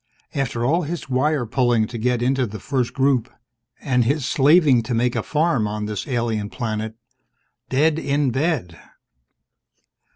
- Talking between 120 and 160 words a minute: Yes, average, 150 wpm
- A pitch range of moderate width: Yes, average, 3.7 semitones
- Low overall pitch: Yes, low, 125 Hz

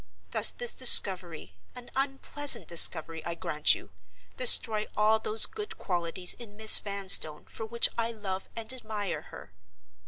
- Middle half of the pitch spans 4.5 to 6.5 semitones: Yes, wide, 5.5 semitones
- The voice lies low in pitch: No, high, 205 Hz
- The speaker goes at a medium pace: No, slow, 130 wpm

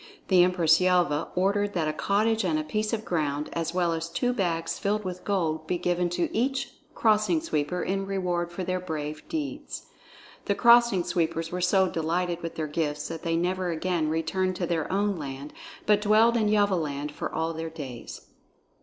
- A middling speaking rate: Yes, average, 185 wpm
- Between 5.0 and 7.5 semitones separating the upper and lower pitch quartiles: No, average, 3.7 semitones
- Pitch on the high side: No, medium, 180 Hz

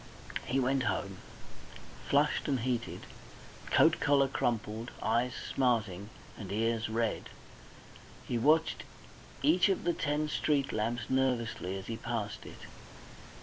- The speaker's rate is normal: No, slow, 120 wpm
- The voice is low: Yes, low, 120 Hz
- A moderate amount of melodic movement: Yes, average, 3.7 semitones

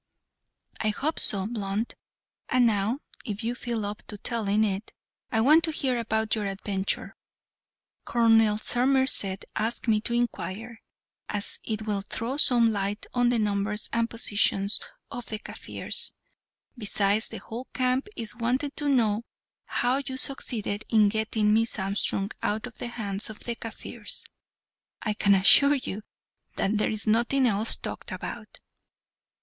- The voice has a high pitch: Yes, high, 220 Hz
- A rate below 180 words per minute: Yes, average, 150 wpm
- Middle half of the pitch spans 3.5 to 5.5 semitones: No, average, 2.7 semitones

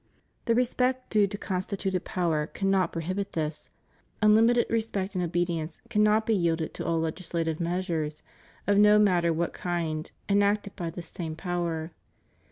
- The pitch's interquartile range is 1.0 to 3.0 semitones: No, average, 3.7 semitones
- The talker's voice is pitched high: No, medium, 180 Hz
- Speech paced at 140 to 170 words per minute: Yes, average, 150 wpm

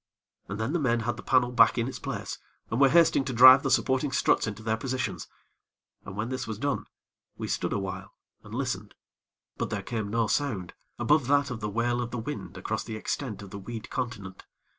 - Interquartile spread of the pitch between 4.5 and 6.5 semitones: No, average, 3.3 semitones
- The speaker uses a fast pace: Yes, fast, 210 wpm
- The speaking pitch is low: Yes, low, 120 Hz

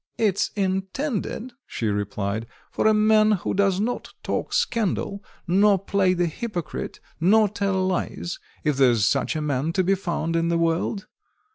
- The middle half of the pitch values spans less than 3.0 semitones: No, average, 4.0 semitones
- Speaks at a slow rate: No, average, 155 wpm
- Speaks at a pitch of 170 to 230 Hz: Yes, high, 190 Hz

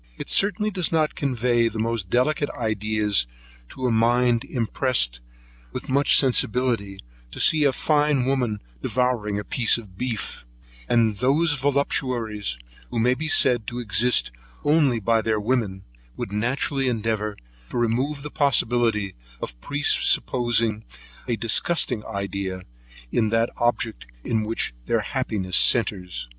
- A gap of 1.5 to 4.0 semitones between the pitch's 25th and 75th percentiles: Yes, average, 3.5 semitones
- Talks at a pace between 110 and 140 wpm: Yes, slow, 135 wpm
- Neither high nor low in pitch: No, low, 115 Hz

